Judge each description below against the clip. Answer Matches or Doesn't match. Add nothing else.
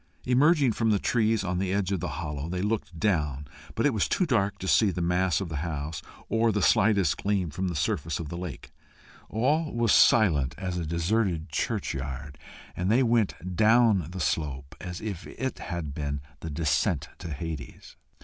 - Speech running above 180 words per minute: Matches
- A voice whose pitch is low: Matches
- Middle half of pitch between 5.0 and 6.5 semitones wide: Matches